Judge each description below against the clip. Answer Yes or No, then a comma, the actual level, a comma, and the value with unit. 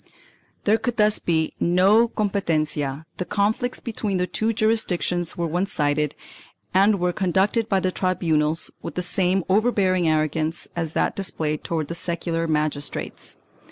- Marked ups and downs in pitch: No, average, 4.0 semitones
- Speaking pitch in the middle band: Yes, medium, 180 Hz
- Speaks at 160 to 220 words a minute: No, average, 145 wpm